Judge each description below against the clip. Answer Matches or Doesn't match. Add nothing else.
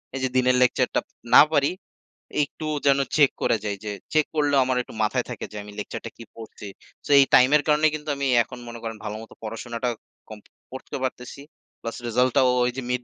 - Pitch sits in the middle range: Doesn't match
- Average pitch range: Matches